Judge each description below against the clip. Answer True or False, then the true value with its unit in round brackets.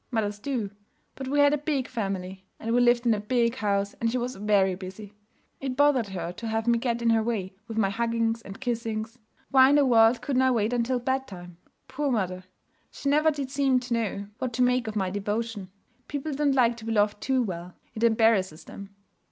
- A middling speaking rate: False (215 wpm)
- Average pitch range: True (3.8 semitones)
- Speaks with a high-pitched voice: True (230 Hz)